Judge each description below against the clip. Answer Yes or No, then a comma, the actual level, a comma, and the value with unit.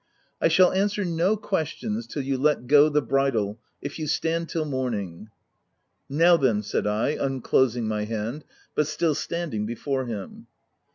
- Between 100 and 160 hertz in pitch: Yes, medium, 140 Hz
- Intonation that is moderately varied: No, wide, 6.1 semitones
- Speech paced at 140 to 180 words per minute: Yes, average, 170 wpm